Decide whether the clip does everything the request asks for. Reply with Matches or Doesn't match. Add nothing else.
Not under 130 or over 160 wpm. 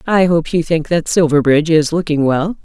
Doesn't match